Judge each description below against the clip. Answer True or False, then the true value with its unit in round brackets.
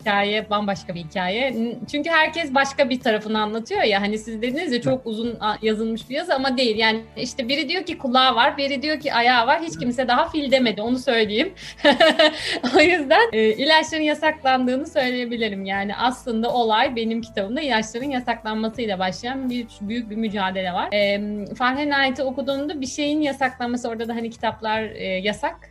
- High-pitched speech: True (245 Hz)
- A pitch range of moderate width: True (4.1 semitones)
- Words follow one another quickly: True (170 wpm)